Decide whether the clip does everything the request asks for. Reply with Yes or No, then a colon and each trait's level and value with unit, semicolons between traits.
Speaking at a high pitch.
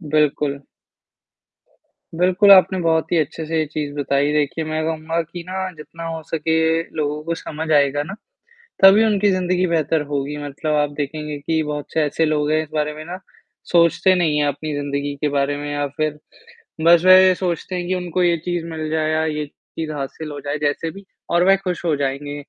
No: medium, 155 Hz